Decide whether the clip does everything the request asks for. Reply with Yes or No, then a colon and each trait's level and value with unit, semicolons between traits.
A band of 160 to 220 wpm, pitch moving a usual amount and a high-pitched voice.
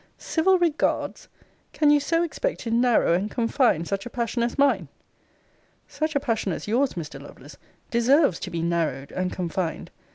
No: average, 165 wpm; wide, 8.7 semitones; high, 230 Hz